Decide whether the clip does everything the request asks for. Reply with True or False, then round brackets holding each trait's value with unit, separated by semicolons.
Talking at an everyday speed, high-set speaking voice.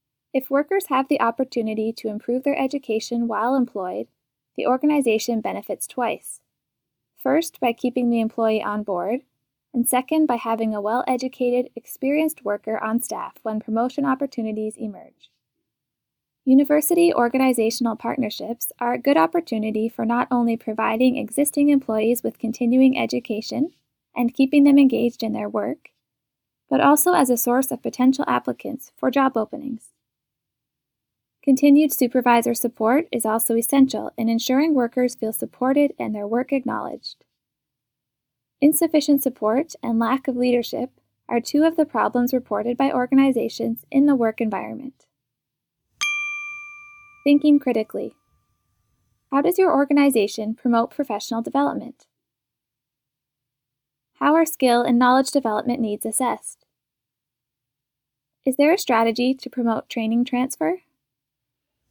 False (125 wpm; 245 Hz)